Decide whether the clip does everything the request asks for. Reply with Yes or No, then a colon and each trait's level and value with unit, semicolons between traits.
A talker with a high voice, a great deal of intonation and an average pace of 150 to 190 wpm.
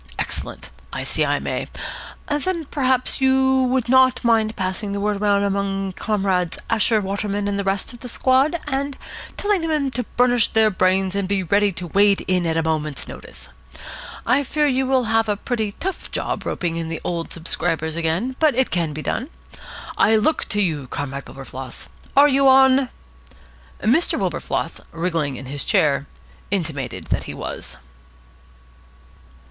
Yes: high, 205 Hz; wide, 7.0 semitones; average, 165 wpm